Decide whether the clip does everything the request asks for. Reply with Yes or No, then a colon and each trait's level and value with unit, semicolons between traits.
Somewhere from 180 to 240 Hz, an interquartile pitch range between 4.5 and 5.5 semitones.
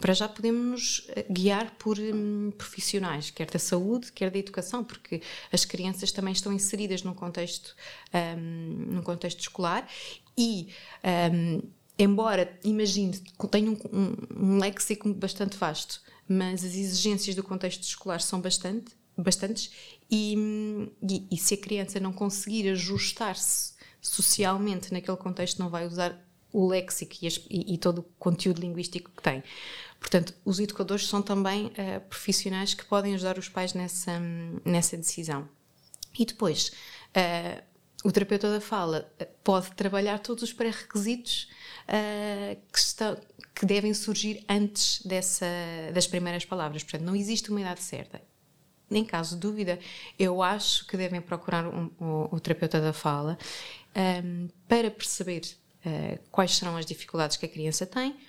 No: high, 190 Hz; average, 2.8 semitones